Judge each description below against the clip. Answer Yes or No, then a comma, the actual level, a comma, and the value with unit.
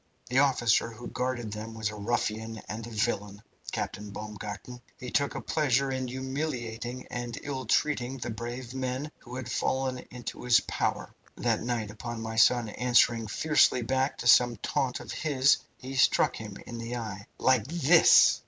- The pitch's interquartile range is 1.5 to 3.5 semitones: Yes, average, 2.7 semitones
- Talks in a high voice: No, low, 120 Hz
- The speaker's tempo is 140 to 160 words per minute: No, average, 170 wpm